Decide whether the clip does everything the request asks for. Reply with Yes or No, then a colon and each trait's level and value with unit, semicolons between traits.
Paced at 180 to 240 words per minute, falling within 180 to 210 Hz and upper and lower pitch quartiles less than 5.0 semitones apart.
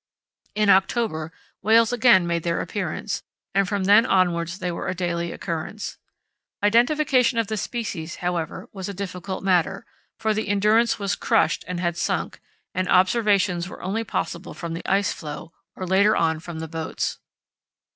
No: average, 160 wpm; high, 190 Hz; average, 3.7 semitones